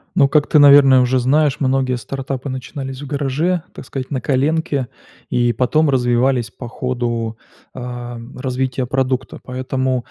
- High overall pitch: No, low, 130 Hz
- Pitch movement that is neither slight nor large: No, narrow, 1.8 semitones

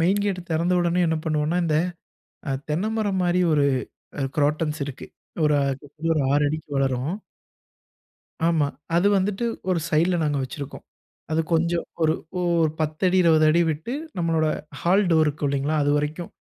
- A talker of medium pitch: Yes, medium, 160 Hz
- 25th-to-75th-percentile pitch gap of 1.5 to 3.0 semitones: Yes, average, 2.7 semitones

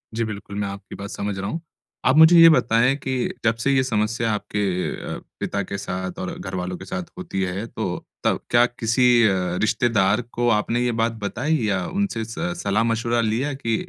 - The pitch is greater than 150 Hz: No, low, 115 Hz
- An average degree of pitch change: Yes, average, 3.7 semitones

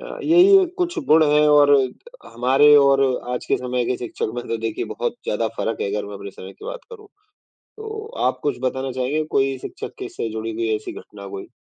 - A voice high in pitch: No, low, 130 Hz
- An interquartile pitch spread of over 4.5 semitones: Yes, wide, 5.4 semitones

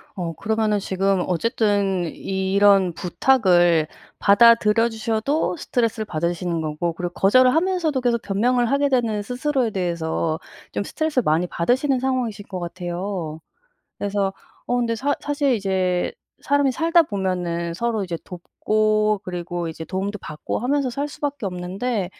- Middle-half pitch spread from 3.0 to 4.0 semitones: No, wide, 5.6 semitones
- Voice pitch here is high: Yes, high, 205 Hz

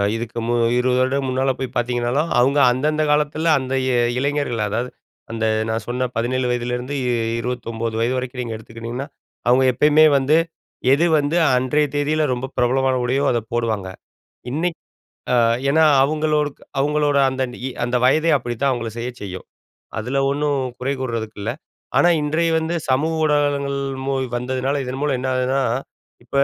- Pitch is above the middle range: No, low, 130 Hz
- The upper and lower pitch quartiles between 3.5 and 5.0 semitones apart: No, average, 3.1 semitones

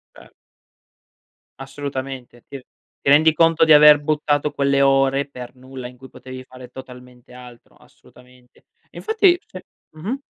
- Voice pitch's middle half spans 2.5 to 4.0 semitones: Yes, average, 2.8 semitones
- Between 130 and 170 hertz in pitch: Yes, low, 135 Hz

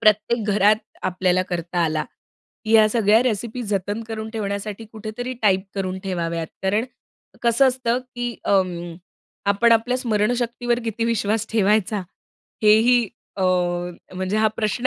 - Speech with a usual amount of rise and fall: Yes, average, 3.1 semitones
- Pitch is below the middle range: No, high, 215 Hz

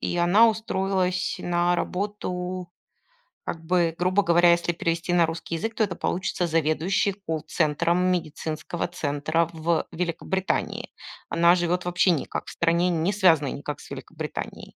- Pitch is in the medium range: Yes, medium, 175 Hz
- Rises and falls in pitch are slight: Yes, narrow, 1.8 semitones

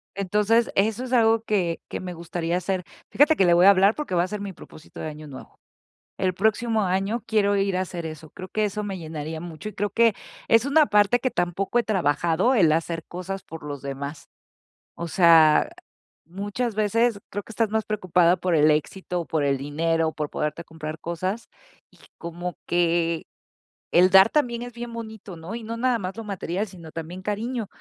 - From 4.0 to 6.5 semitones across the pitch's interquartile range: Yes, average, 4.6 semitones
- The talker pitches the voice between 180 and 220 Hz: Yes, medium, 185 Hz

